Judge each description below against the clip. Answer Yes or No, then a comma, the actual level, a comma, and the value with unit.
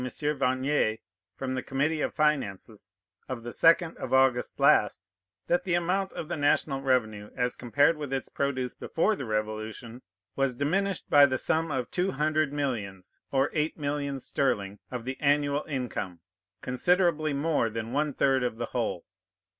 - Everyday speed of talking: Yes, average, 160 wpm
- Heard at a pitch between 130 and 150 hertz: Yes, low, 135 Hz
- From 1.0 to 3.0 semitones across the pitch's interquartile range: No, average, 3.7 semitones